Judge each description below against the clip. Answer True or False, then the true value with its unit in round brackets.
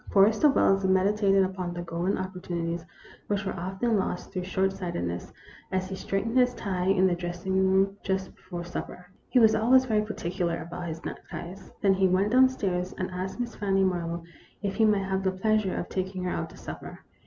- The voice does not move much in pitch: True (2.0 semitones)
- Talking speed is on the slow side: False (200 wpm)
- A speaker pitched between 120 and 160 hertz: False (190 Hz)